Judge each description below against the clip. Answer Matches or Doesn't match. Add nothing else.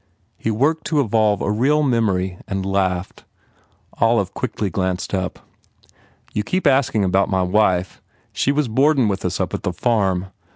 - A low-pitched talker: Matches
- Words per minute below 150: Doesn't match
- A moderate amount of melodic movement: Matches